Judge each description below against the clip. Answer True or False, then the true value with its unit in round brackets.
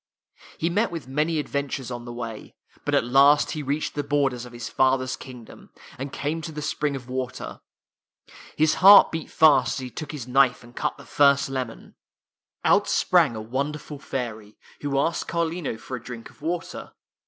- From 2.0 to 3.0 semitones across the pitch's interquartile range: False (3.4 semitones)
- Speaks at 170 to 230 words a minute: True (185 wpm)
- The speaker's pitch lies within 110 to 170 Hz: True (140 Hz)